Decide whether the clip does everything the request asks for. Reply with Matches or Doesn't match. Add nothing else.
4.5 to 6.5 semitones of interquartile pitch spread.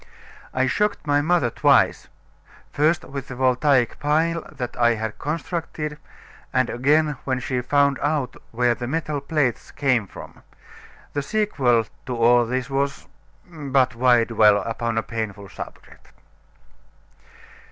Doesn't match